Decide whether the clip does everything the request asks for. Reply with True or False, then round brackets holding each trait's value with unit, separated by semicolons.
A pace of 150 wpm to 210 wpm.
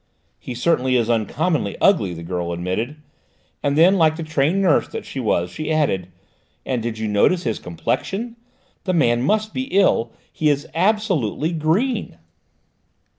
True (155 wpm)